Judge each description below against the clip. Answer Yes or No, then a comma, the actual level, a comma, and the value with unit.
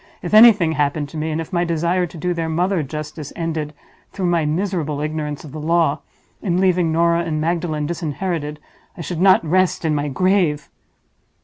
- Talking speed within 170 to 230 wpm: Yes, average, 185 wpm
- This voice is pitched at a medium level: Yes, medium, 165 Hz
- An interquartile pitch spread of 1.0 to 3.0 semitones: Yes, narrow, 2.6 semitones